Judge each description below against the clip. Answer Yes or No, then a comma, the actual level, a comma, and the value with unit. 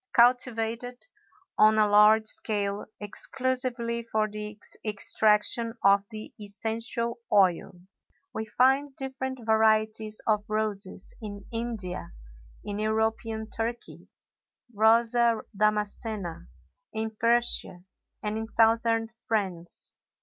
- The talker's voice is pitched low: No, high, 220 Hz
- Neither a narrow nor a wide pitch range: No, narrow, 1.8 semitones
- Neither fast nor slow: No, slow, 95 wpm